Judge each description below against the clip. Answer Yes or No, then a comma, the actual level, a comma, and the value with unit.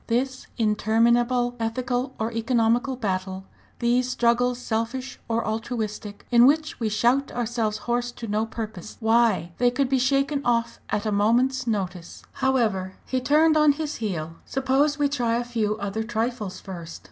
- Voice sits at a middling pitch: No, high, 235 Hz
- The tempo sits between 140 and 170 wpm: Yes, average, 155 wpm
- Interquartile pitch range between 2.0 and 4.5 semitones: Yes, average, 2.8 semitones